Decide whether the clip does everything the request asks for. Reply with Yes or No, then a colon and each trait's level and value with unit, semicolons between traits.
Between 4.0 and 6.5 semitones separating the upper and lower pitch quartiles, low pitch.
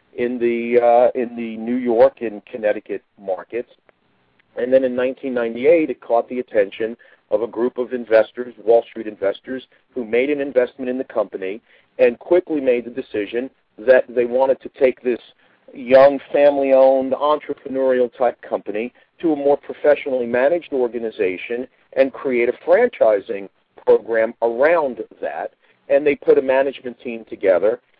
No: narrow, 2.5 semitones; low, 125 Hz